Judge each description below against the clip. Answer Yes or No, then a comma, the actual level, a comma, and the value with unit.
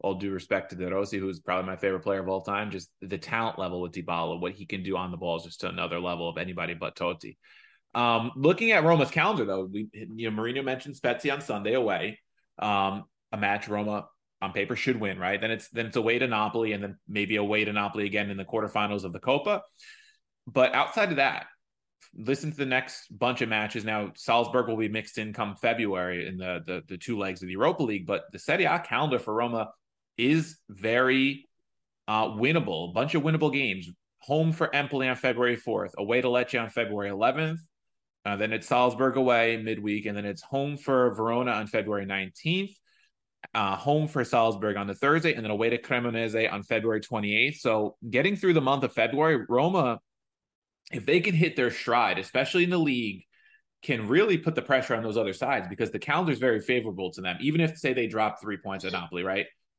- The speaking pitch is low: Yes, low, 110 Hz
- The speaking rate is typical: No, fast, 215 wpm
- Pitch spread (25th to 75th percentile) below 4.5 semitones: No, average, 4.9 semitones